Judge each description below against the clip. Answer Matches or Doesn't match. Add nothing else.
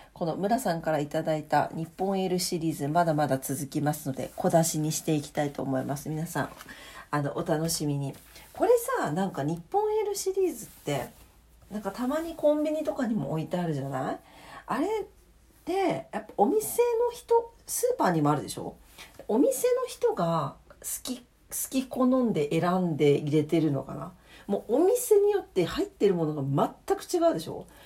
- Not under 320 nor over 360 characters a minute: Matches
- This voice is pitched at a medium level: Matches